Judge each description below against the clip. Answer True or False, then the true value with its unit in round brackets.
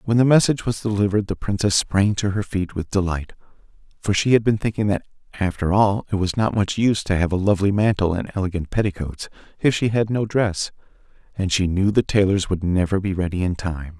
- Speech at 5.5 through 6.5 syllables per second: True (5.9 syllables/s)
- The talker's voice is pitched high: False (100 Hz)